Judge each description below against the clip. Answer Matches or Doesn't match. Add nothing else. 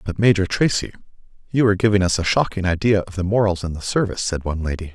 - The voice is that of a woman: Doesn't match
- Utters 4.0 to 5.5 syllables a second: Doesn't match